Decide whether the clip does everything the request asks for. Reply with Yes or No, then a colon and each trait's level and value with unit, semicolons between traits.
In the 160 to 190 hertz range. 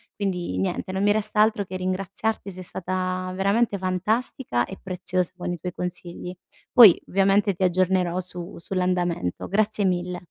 Yes: medium, 185 Hz